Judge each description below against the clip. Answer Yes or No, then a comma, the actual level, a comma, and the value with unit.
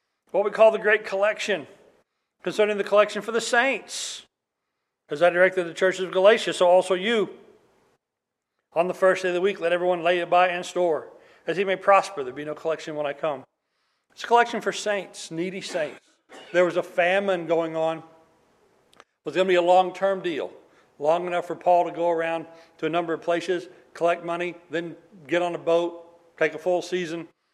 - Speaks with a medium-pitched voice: Yes, medium, 180 Hz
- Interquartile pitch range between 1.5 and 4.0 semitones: Yes, average, 2.7 semitones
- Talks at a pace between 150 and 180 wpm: No, average, 200 wpm